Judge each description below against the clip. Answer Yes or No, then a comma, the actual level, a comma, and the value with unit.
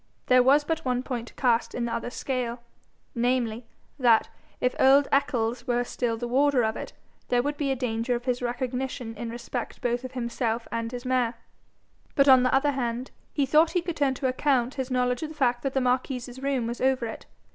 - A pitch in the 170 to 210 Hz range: No, very high, 250 Hz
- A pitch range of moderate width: No, narrow, 2.0 semitones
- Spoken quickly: Yes, fast, 210 wpm